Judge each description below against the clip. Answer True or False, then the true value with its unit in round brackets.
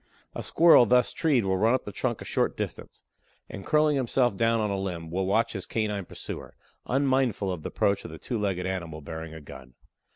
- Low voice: True (100 Hz)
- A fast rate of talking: True (215 wpm)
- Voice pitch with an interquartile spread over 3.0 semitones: True (5.2 semitones)